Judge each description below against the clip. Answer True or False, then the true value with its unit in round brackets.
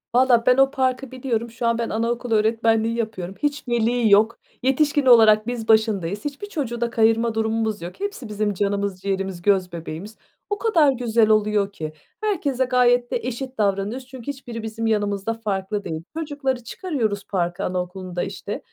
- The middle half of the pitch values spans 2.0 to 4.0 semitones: True (3.7 semitones)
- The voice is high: True (225 Hz)